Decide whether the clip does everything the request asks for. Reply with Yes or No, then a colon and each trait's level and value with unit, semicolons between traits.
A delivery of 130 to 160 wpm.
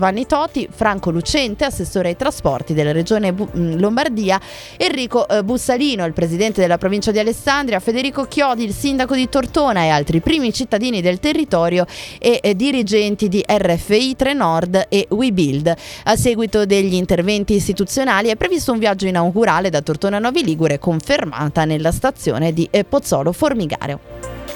Yes: average, 140 wpm